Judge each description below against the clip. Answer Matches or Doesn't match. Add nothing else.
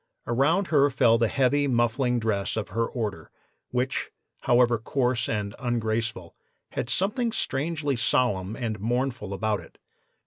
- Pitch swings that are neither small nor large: Matches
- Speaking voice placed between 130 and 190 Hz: Doesn't match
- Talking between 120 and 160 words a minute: Matches